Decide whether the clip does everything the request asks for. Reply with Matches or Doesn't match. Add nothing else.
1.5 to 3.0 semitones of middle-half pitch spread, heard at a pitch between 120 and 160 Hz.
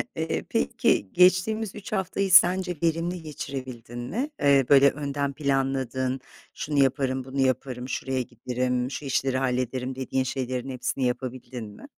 Matches